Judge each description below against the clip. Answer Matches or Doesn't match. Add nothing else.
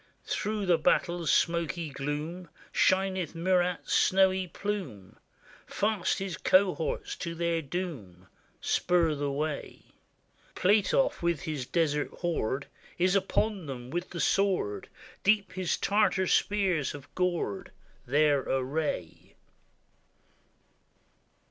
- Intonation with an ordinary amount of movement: Matches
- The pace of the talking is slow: Matches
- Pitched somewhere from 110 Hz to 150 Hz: Doesn't match